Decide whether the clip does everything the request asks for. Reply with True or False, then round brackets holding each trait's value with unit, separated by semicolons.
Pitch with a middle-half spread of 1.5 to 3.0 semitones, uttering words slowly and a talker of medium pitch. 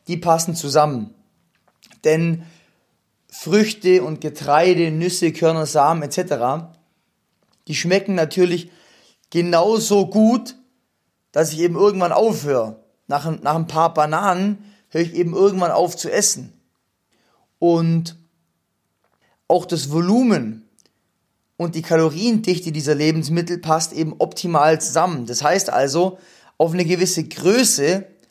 True (2.7 semitones; 115 wpm; 170 Hz)